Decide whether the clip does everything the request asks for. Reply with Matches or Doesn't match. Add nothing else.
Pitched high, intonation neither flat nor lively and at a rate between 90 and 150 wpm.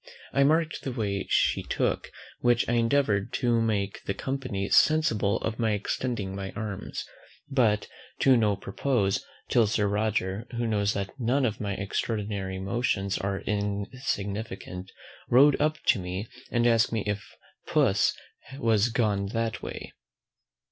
Doesn't match